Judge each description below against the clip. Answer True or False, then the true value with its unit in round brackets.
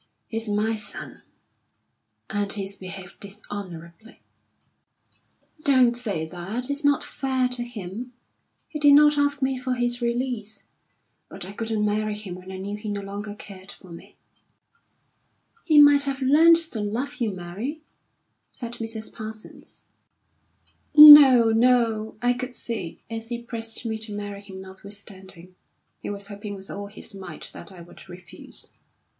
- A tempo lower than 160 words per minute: True (150 wpm)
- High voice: True (220 Hz)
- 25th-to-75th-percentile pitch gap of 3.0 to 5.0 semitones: True (3.9 semitones)